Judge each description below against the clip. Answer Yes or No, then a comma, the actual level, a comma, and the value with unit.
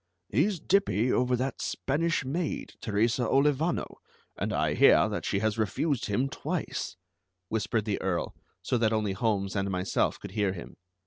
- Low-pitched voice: Yes, low, 115 Hz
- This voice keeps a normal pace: Yes, average, 155 wpm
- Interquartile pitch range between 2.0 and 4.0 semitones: No, average, 5.1 semitones